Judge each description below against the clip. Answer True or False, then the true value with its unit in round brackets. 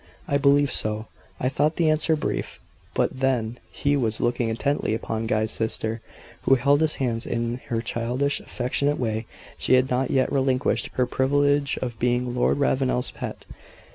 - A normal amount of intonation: True (3.3 semitones)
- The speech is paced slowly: False (165 wpm)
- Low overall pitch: True (130 Hz)